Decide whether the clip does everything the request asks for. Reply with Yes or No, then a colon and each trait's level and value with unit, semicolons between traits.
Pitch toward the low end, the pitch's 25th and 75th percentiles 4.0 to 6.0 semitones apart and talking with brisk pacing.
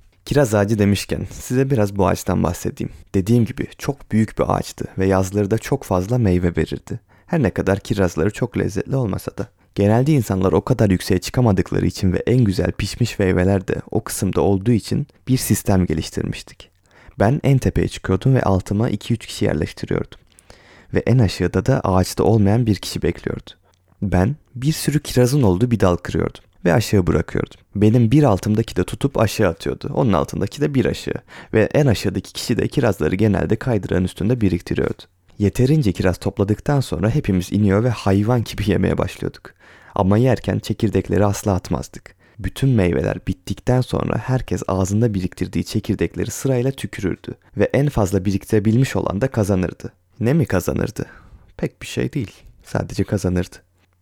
Yes: low, 100 Hz; average, 4.4 semitones; fast, 160 wpm